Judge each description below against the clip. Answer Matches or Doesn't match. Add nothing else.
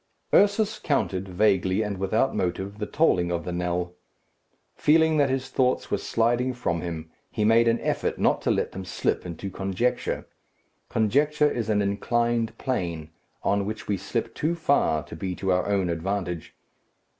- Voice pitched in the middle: Doesn't match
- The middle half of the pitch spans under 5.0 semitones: Doesn't match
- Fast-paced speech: Doesn't match